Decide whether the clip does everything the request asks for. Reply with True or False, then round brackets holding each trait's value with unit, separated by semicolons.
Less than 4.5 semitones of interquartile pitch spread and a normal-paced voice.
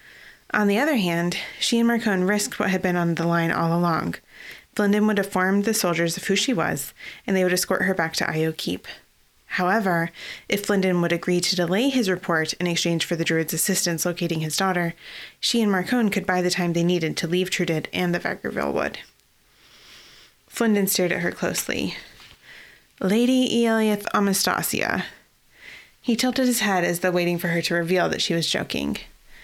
True (3.3 semitones; 185 wpm)